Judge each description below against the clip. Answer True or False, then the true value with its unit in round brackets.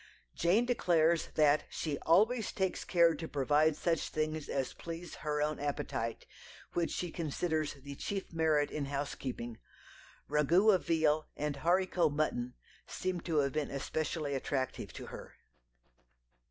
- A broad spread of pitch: False (3.0 semitones)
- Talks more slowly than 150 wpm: True (140 wpm)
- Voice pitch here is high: False (155 Hz)